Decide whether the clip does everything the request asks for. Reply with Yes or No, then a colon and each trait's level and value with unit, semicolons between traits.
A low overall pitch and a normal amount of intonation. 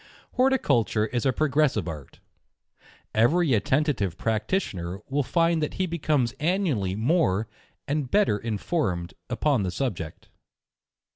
No: low, 130 Hz; wide, 7.3 semitones